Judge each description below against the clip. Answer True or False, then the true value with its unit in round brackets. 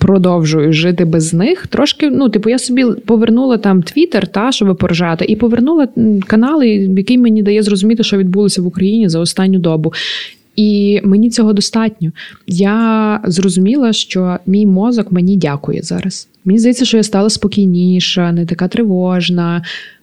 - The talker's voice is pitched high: True (200 Hz)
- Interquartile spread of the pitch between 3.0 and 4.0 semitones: True (3.6 semitones)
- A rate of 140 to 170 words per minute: True (150 wpm)